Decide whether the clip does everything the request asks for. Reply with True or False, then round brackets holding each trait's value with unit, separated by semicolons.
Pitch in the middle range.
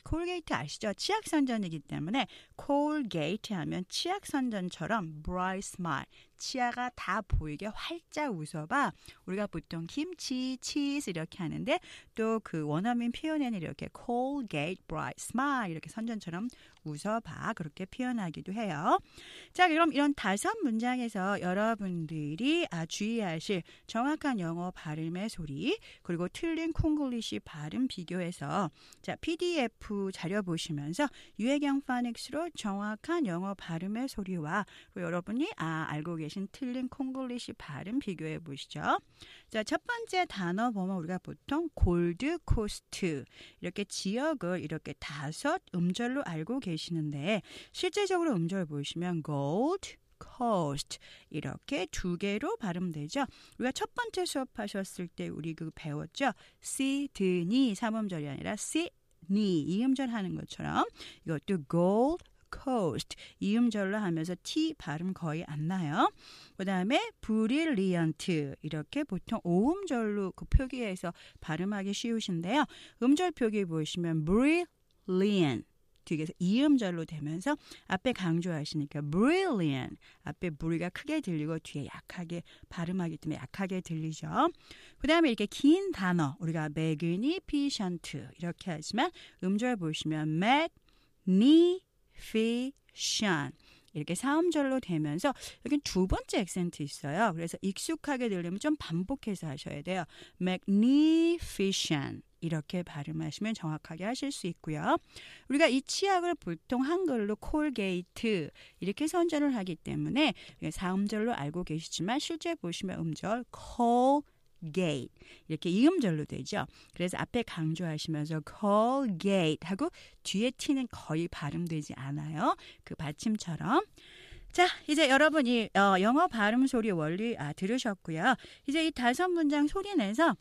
False (200 Hz)